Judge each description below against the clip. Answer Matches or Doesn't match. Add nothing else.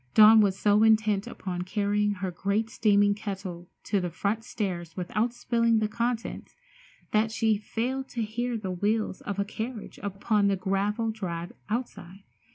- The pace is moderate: Matches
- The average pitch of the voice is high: Matches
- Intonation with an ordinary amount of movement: Doesn't match